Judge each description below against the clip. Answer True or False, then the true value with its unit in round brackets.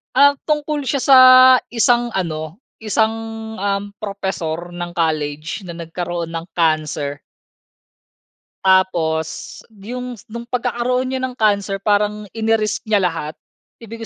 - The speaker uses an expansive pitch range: True (5.9 semitones)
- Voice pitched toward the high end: True (200 Hz)